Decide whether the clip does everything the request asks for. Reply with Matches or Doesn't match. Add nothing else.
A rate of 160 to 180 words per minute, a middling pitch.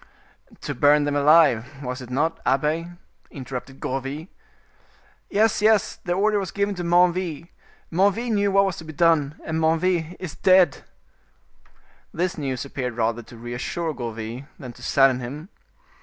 Doesn't match